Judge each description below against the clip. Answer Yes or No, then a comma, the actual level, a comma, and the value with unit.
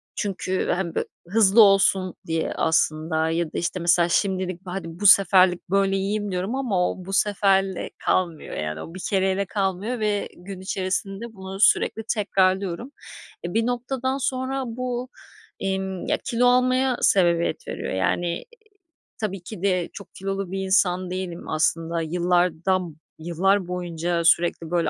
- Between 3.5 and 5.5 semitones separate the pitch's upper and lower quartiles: No, average, 2.7 semitones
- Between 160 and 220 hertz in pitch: Yes, high, 190 Hz